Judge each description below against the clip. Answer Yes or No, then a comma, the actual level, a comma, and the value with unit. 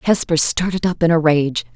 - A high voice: No, medium, 165 Hz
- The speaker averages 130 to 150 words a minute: No, fast, 205 wpm